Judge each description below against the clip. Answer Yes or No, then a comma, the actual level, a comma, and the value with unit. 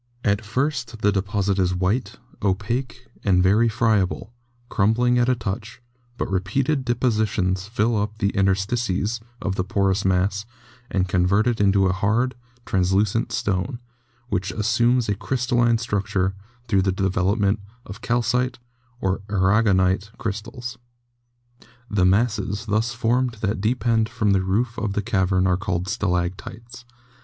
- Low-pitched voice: Yes, low, 105 Hz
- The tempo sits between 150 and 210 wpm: No, average, 140 wpm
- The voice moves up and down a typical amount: Yes, average, 3.6 semitones